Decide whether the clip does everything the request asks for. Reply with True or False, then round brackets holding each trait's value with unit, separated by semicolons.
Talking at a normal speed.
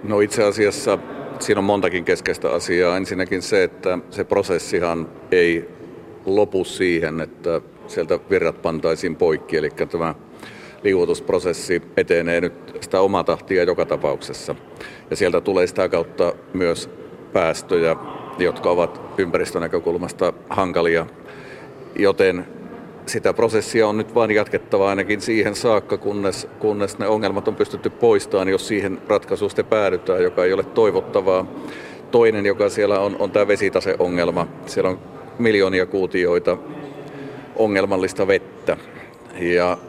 True (120 wpm)